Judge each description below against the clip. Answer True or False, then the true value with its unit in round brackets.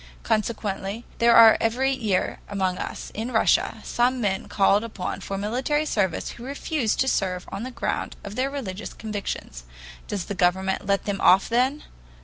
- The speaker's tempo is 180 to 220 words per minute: False (165 wpm)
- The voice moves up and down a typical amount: True (4.0 semitones)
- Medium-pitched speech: False (215 Hz)